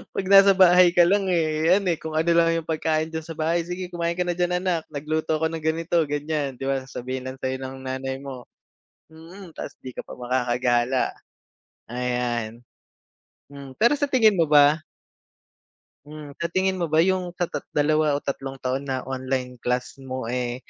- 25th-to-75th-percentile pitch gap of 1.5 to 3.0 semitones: No, average, 4.6 semitones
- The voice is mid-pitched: Yes, medium, 155 Hz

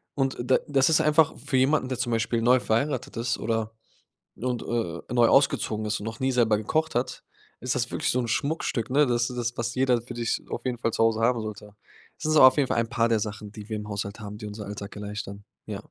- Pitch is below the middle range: Yes, low, 115 Hz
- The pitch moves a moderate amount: Yes, average, 3.1 semitones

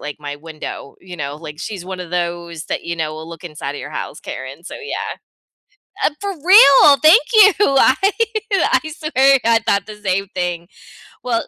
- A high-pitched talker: No, medium, 180 Hz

